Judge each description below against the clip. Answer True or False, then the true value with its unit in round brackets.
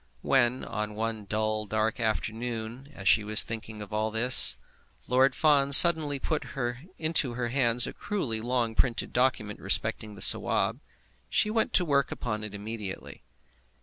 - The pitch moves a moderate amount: True (3.6 semitones)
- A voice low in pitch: True (115 Hz)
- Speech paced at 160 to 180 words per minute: False (150 wpm)